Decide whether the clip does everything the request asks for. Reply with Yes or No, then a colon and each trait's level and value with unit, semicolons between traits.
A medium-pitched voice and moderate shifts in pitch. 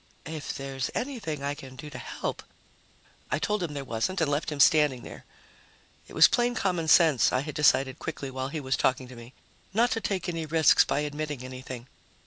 Yes: medium, 145 Hz; average, 3.7 semitones